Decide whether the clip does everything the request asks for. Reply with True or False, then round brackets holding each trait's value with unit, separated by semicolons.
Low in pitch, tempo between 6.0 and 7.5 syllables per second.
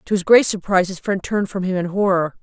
False (190 Hz; 6.5 syllables/s)